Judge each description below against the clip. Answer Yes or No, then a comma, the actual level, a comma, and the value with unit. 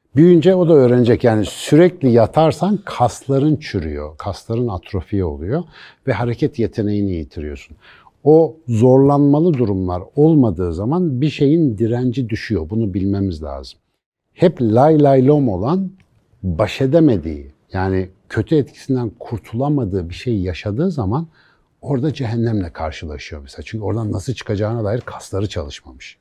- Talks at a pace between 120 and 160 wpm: Yes, average, 125 wpm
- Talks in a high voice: No, low, 115 Hz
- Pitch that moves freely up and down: Yes, wide, 7.0 semitones